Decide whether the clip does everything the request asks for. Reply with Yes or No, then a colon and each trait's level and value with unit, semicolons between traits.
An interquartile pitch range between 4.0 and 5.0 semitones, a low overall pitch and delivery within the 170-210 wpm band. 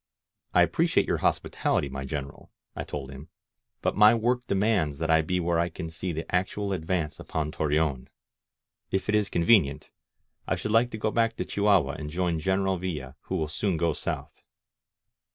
Yes: average, 4.5 semitones; very low, 85 Hz; average, 180 wpm